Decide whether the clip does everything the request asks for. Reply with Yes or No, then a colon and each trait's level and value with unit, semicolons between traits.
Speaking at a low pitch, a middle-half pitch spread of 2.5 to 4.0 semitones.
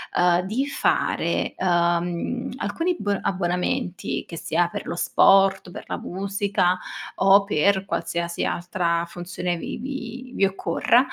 No: medium, 185 Hz; average, 2.8 semitones